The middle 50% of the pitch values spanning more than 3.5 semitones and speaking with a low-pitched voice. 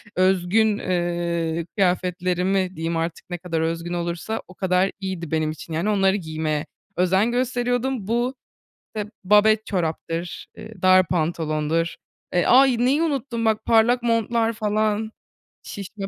No: average, 4.4 semitones; high, 190 Hz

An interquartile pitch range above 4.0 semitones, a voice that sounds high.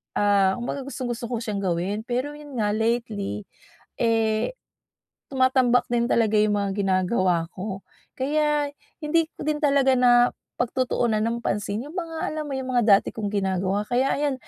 Yes: average, 4.6 semitones; high, 235 Hz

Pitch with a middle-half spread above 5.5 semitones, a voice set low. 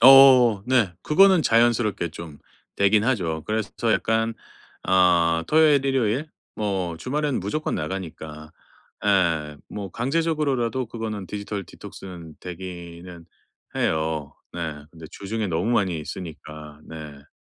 Yes: wide, 6.3 semitones; low, 100 Hz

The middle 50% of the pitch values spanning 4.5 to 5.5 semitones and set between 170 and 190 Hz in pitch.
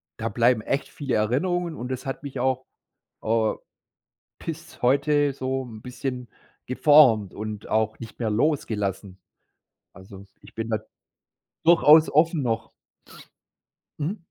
No: average, 4.9 semitones; low, 125 Hz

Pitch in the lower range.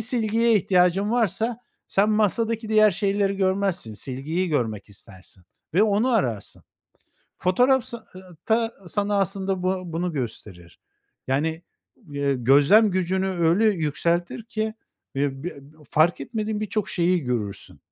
No: medium, 185 Hz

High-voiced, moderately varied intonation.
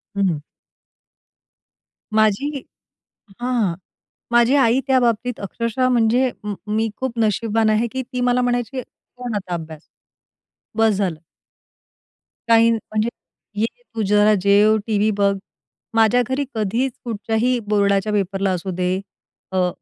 Yes: high, 220 Hz; average, 3.4 semitones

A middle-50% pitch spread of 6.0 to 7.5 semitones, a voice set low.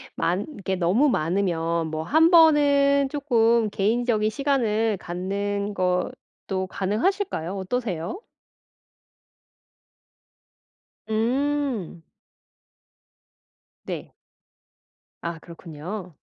No: wide, 6.9 semitones; high, 210 Hz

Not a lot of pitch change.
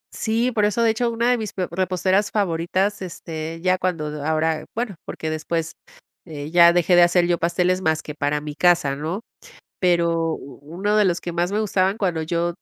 No: average, 3.3 semitones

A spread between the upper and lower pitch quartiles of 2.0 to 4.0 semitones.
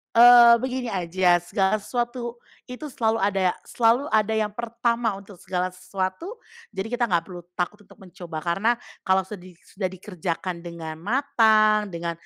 No: average, 4.5 semitones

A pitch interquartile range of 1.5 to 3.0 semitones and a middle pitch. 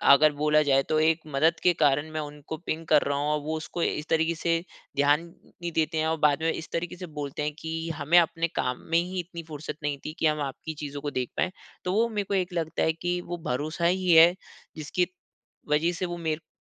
Yes: narrow, 2.4 semitones; medium, 160 Hz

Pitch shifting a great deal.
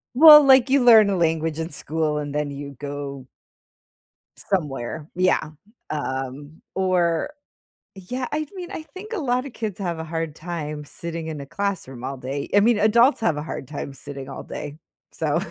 Yes: wide, 7.2 semitones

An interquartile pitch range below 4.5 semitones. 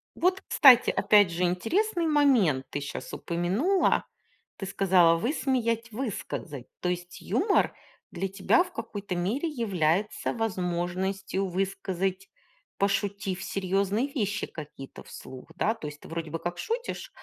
No: average, 4.9 semitones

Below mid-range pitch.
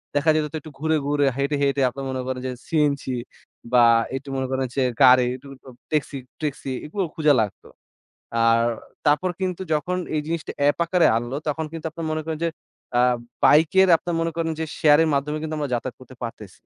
No: medium, 145 Hz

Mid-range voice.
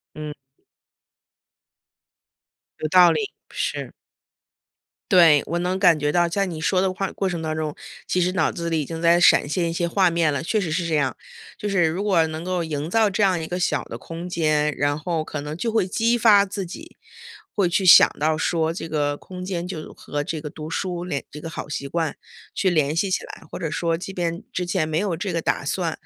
Yes: medium, 170 Hz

